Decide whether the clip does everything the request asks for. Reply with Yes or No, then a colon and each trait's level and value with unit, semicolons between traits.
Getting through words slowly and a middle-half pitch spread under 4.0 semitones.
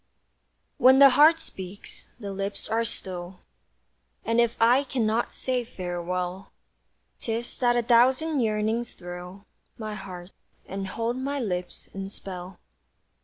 No: slow, 125 wpm; average, 4.3 semitones